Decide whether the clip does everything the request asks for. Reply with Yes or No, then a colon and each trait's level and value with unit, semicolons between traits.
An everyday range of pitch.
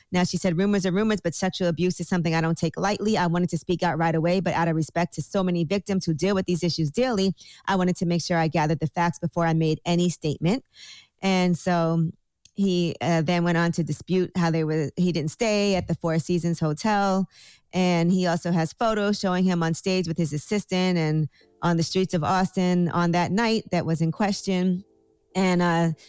No: narrow, 2.2 semitones